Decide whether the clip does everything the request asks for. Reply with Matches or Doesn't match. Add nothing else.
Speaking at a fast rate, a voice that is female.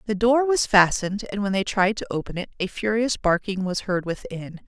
Matches